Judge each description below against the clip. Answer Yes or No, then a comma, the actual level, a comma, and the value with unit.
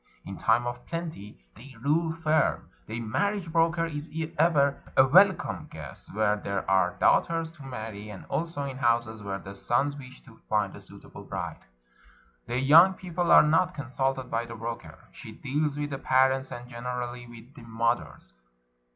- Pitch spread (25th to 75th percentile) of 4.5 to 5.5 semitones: Yes, average, 5.2 semitones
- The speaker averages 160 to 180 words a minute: Yes, average, 170 wpm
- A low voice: Yes, low, 130 Hz